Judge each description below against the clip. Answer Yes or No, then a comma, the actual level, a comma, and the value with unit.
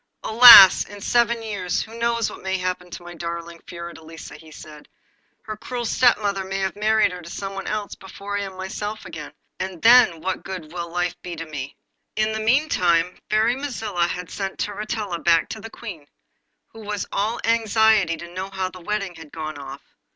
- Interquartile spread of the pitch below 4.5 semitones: Yes, average, 4.1 semitones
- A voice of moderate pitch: No, high, 195 Hz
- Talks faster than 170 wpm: Yes, average, 190 wpm